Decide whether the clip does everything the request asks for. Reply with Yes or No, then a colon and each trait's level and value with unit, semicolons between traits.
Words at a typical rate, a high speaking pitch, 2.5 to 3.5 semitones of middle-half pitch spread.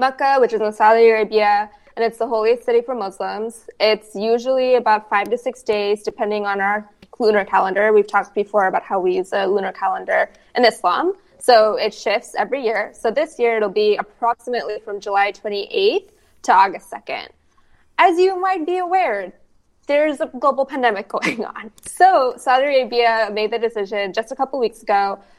No: average, 180 wpm; high, 225 Hz; average, 4.2 semitones